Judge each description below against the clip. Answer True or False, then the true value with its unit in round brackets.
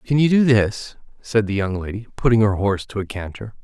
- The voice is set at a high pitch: False (110 Hz)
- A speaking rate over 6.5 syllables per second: False (5.7 syllables/s)